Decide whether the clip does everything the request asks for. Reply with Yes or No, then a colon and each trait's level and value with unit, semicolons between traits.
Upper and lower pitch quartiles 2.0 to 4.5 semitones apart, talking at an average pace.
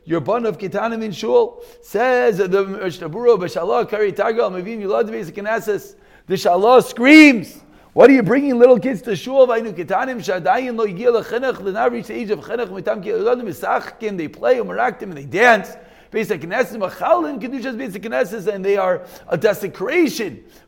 Yes: average, 4.2 semitones; average, 180 wpm